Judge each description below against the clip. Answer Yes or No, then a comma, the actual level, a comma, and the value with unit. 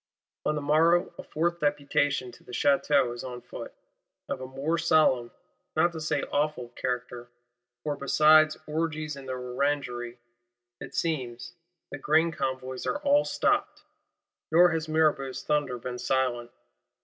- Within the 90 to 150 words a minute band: Yes, average, 145 wpm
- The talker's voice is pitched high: No, medium, 145 Hz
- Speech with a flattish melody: No, average, 3.7 semitones